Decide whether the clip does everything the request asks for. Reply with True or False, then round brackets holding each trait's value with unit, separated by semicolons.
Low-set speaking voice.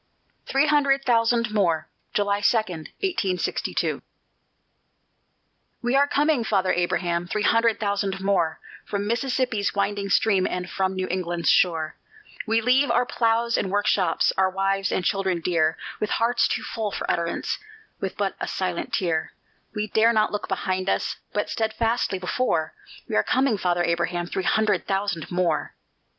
False (200 Hz)